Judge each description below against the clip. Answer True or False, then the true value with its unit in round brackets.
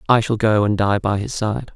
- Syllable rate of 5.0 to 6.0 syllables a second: True (5.1 syllables/s)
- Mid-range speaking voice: False (105 Hz)